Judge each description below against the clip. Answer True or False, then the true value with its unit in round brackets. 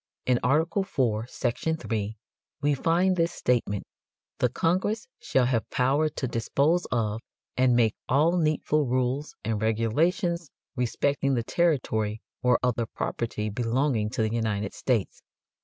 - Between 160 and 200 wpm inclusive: False (135 wpm)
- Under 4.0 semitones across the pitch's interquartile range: False (5.4 semitones)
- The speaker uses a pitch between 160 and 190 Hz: False (125 Hz)